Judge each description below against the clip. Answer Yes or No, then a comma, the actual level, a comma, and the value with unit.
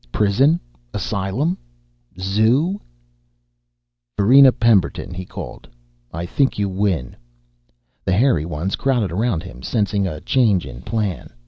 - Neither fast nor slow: No, slow, 115 wpm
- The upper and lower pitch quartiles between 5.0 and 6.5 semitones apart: Yes, average, 5.3 semitones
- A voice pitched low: Yes, low, 100 Hz